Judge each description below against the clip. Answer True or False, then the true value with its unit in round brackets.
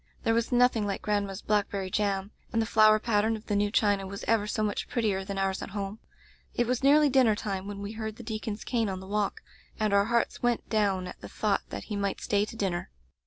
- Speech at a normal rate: False (235 wpm)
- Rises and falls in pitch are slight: True (2.2 semitones)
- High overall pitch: True (210 Hz)